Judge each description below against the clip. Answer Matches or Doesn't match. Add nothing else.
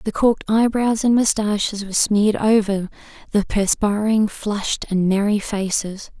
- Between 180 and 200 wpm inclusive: Doesn't match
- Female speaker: Matches